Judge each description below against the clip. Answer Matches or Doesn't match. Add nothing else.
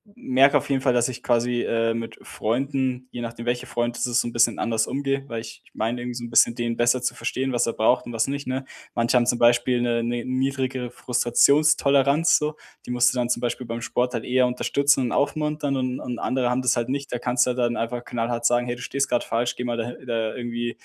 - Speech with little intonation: Matches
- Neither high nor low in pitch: Doesn't match